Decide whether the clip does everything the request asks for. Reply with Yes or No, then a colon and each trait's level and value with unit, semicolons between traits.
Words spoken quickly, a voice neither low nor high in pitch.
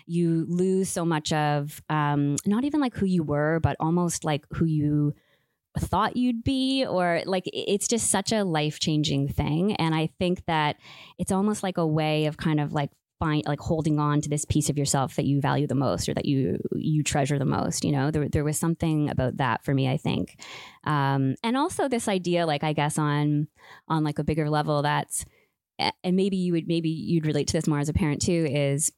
Yes: fast, 215 wpm; medium, 155 Hz